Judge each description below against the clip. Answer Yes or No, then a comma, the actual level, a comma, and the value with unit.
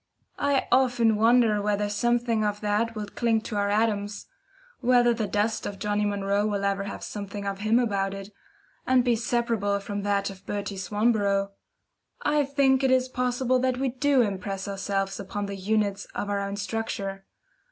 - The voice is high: Yes, high, 210 Hz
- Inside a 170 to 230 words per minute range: Yes, average, 175 wpm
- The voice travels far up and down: No, average, 3.1 semitones